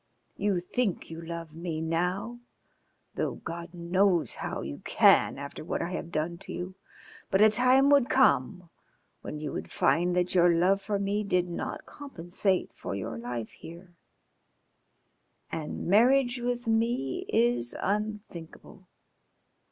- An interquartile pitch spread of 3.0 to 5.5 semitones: Yes, average, 4.2 semitones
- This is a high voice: No, medium, 180 Hz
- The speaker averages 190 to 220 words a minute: No, average, 140 wpm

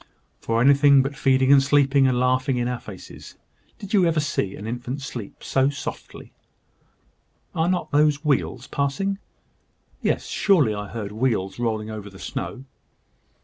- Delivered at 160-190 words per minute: No, average, 150 wpm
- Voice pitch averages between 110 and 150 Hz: Yes, low, 135 Hz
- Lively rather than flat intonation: No, average, 4.0 semitones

